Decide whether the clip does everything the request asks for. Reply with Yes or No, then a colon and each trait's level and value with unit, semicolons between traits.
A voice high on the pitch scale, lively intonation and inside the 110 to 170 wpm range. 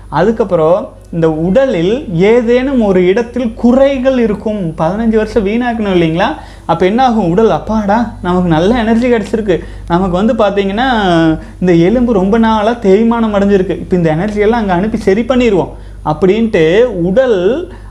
No: high, 210 Hz; average, 4.6 semitones; fast, 130 wpm